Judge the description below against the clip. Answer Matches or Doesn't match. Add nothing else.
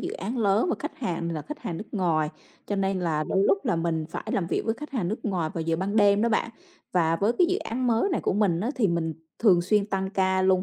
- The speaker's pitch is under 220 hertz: Matches